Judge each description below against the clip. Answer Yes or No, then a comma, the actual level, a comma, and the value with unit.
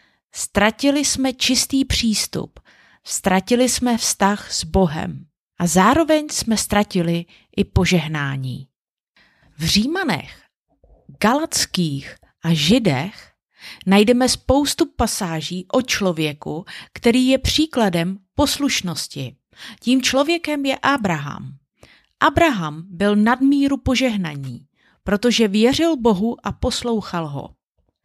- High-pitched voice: Yes, high, 210 Hz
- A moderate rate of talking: No, slow, 90 wpm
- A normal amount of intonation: No, wide, 7.2 semitones